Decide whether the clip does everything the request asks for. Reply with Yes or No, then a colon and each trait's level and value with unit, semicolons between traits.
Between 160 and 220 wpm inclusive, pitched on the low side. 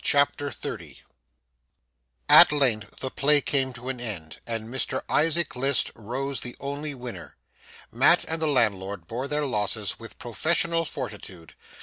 No: average, 140 wpm; low, 130 Hz